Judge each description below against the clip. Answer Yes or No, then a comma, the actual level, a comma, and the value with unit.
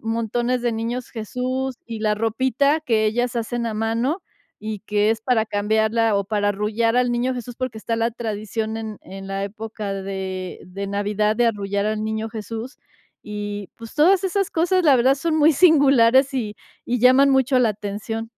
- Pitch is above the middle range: Yes, high, 225 Hz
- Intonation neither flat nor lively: Yes, average, 3.2 semitones